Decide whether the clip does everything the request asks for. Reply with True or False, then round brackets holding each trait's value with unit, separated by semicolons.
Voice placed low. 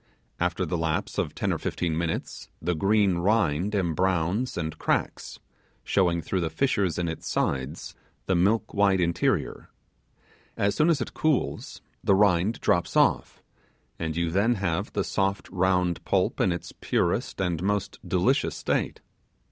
True (90 Hz)